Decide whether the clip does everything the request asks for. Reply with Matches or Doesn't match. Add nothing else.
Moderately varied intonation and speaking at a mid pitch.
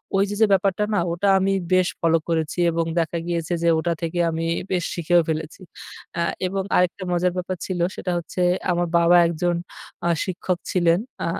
Doesn't match